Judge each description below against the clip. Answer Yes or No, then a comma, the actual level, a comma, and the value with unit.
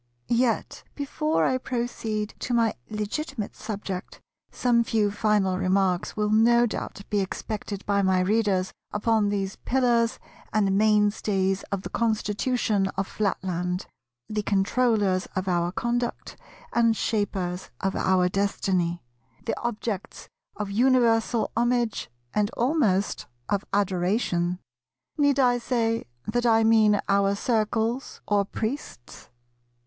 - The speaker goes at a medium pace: No, slow, 120 wpm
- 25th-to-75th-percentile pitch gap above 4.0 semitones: No, average, 3.3 semitones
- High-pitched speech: Yes, high, 210 Hz